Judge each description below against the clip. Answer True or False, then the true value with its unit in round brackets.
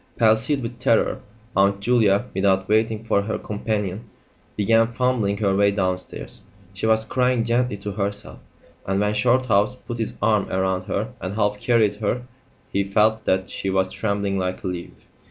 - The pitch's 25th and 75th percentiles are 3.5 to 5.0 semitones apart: False (2.5 semitones)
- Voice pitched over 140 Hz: False (105 Hz)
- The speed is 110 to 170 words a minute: True (165 wpm)